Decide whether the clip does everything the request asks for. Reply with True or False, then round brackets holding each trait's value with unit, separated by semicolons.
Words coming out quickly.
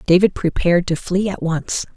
False (185 wpm)